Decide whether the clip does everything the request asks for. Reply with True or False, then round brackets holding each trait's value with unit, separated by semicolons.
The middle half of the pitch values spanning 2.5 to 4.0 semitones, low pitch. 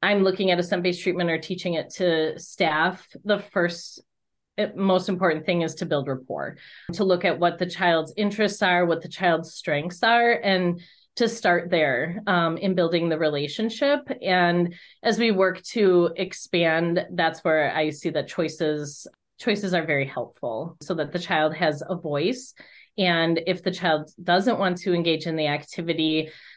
False (2.9 semitones; 175 Hz)